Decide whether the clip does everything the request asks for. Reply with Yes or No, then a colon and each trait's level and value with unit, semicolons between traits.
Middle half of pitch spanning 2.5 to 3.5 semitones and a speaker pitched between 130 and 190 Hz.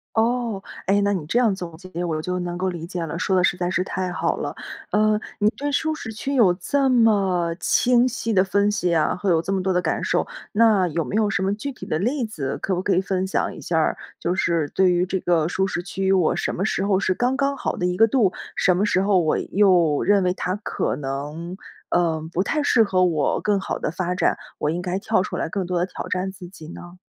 Yes: average, 2.9 semitones; medium, 185 Hz